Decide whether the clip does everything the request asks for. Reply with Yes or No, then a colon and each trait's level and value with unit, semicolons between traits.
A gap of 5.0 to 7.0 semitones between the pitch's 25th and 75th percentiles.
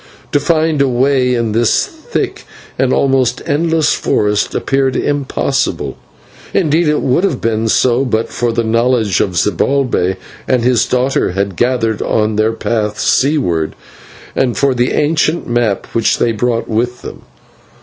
No: average, 3.7 semitones